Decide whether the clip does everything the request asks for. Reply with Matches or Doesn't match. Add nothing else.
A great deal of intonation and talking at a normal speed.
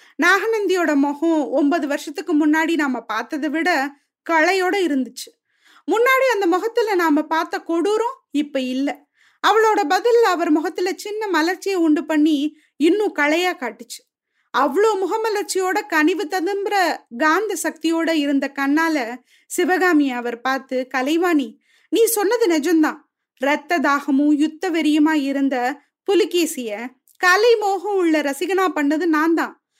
Doesn't match